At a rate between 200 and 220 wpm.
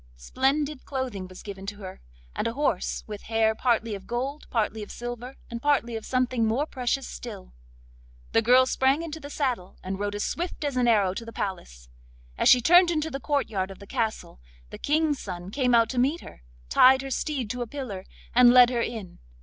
Yes: fast, 205 wpm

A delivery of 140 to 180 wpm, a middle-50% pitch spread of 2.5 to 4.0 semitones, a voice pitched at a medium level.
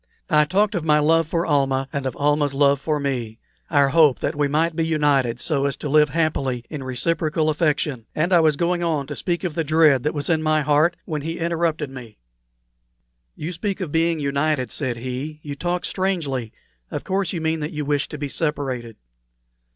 No: fast, 205 wpm; average, 2.8 semitones; medium, 150 Hz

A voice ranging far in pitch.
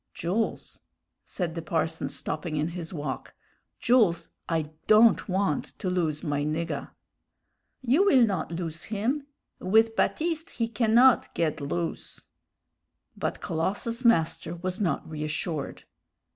Yes: wide, 5.8 semitones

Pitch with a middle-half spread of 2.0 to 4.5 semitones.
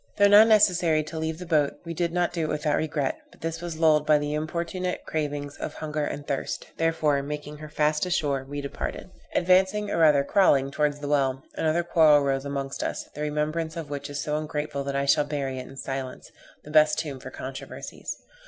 Yes: narrow, 2.4 semitones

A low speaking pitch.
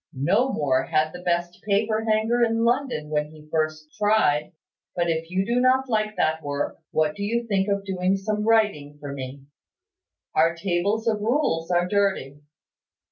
No: high, 190 Hz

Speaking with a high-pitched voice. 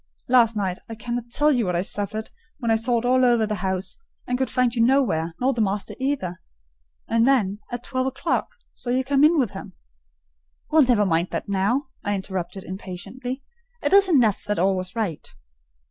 Yes: high, 230 Hz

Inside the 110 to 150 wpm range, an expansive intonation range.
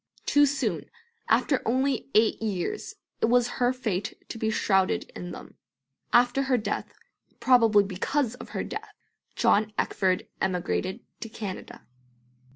No: slow, 135 wpm; average, 4.0 semitones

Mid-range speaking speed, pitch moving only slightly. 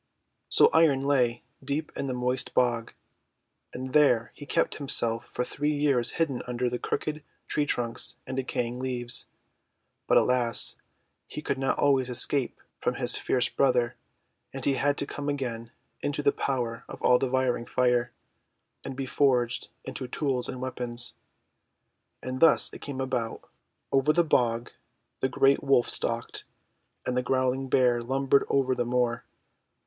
Yes: average, 155 wpm; narrow, 2.1 semitones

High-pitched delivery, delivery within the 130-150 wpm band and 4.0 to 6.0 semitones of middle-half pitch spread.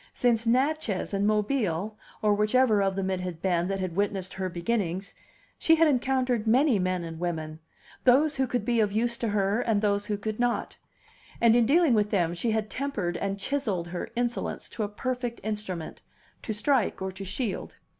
No: high, 210 Hz; average, 190 wpm; average, 4.3 semitones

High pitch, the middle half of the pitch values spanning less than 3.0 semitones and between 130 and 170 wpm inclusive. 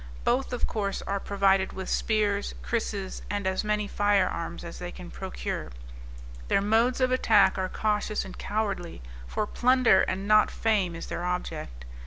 Yes: high, 200 Hz; narrow, 2.4 semitones; average, 165 wpm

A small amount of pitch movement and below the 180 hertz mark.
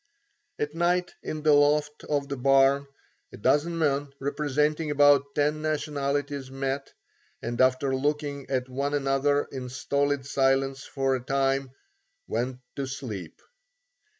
Yes: narrow, 1.6 semitones; medium, 140 Hz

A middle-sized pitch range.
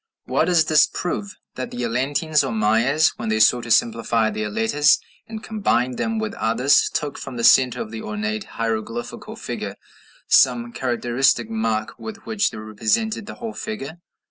No: wide, 5.9 semitones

